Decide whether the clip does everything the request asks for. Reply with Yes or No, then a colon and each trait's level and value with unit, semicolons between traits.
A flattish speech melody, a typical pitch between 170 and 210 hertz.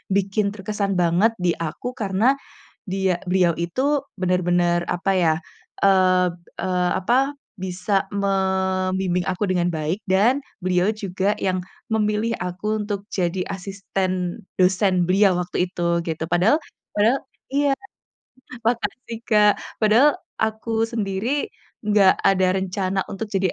Yes: narrow, 2.3 semitones; high, 190 Hz